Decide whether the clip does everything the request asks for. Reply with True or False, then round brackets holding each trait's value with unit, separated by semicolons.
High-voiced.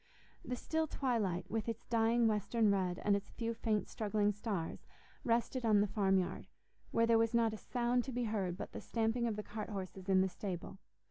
True (220 Hz)